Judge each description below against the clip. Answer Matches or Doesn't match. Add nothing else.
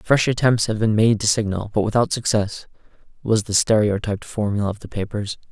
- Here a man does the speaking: Matches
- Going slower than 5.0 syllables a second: Doesn't match